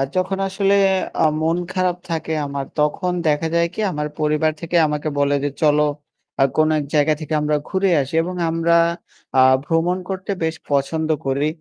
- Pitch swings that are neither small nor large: Yes, average, 3.0 semitones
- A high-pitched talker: No, medium, 160 Hz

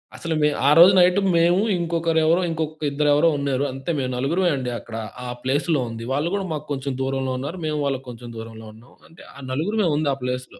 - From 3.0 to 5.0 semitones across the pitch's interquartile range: Yes, average, 4.2 semitones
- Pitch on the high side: No, medium, 145 Hz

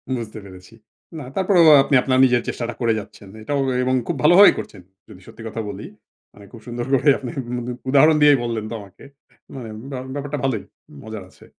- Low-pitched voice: Yes, low, 120 Hz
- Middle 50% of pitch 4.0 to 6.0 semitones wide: Yes, average, 4.3 semitones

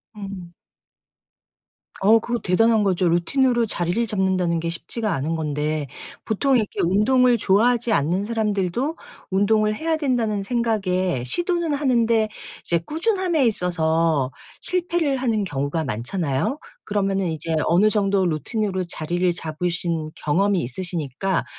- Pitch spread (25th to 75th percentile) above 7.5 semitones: No, wide, 5.5 semitones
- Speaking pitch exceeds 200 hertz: No, high, 195 Hz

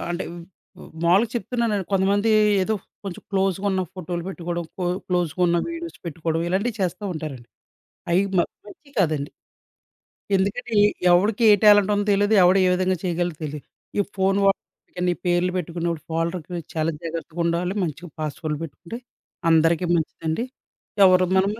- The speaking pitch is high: No, medium, 180 Hz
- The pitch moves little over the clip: No, average, 3.0 semitones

